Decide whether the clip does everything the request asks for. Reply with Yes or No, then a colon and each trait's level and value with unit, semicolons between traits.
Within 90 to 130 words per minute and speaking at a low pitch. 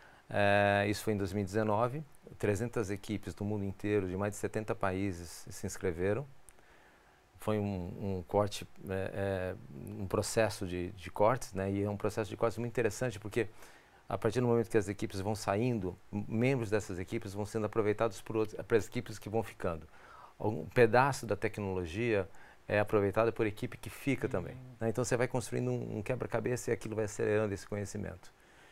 No: average, 180 wpm; low, 105 Hz